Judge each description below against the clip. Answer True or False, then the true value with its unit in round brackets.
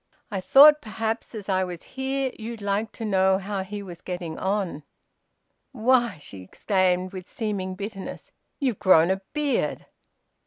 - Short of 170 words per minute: True (150 wpm)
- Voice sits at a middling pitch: False (200 Hz)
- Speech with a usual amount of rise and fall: True (3.3 semitones)